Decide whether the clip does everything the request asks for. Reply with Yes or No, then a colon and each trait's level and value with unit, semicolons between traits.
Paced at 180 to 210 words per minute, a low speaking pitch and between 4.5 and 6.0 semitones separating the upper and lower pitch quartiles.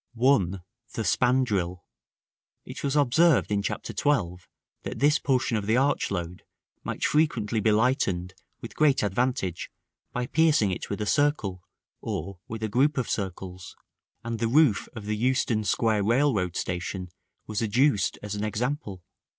No: average, 150 wpm; low, 110 Hz; average, 5.1 semitones